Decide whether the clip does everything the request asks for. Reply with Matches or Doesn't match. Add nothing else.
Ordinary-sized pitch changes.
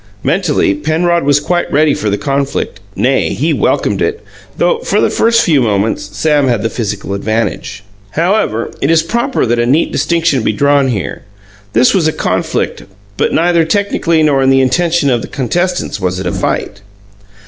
Doesn't match